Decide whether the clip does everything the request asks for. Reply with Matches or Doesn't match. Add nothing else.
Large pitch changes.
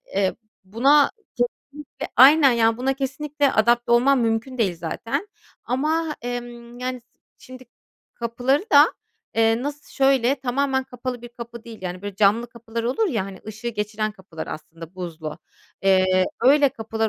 Doesn't match